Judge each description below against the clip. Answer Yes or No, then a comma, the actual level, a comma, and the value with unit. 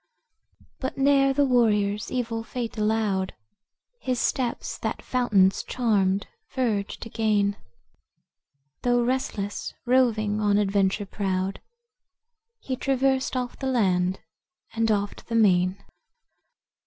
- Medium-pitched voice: No, high, 220 Hz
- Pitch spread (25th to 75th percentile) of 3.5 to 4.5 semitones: Yes, average, 3.9 semitones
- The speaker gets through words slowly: Yes, slow, 105 wpm